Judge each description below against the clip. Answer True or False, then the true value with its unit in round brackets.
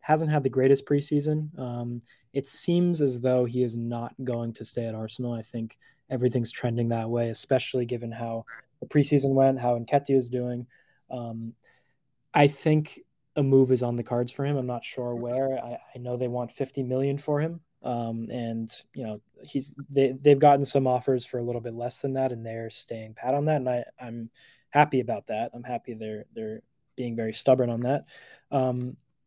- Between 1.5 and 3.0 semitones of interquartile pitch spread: True (2.7 semitones)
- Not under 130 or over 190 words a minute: False (200 wpm)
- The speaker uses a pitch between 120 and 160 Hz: True (125 Hz)